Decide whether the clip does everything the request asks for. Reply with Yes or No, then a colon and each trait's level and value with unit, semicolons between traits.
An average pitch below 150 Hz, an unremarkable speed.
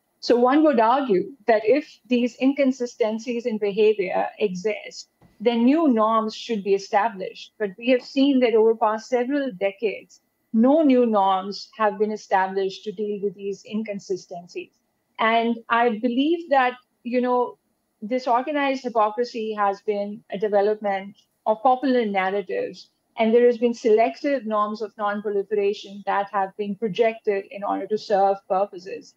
No: high, 220 Hz; average, 145 wpm